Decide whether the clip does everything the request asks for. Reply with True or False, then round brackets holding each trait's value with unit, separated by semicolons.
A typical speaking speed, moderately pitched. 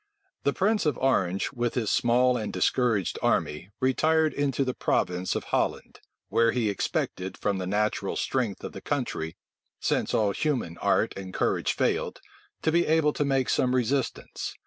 False (165 wpm; 125 Hz)